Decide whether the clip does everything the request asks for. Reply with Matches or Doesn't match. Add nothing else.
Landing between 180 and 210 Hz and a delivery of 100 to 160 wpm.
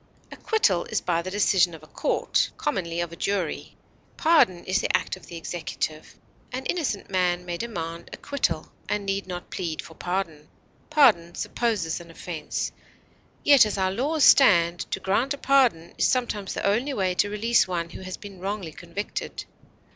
Doesn't match